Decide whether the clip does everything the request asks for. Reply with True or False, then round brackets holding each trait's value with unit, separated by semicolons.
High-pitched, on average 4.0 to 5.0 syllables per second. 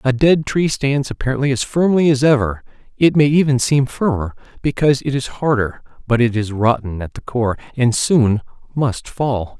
False (130 Hz; 4.9 syllables/s)